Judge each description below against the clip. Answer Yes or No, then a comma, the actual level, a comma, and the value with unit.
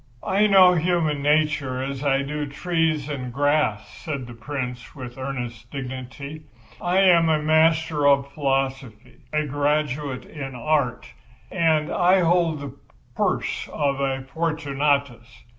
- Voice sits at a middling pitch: Yes, medium, 145 Hz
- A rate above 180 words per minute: No, slow, 135 wpm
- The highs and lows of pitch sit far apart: No, average, 2.9 semitones